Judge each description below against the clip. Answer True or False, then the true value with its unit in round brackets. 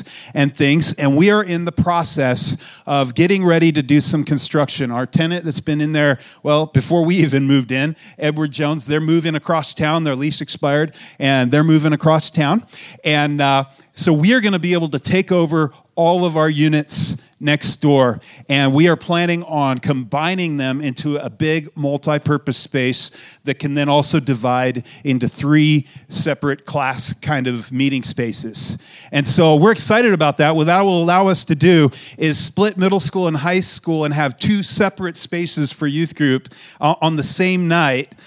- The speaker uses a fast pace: False (185 wpm)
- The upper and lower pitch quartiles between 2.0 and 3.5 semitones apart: True (3.0 semitones)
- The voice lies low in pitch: False (150 Hz)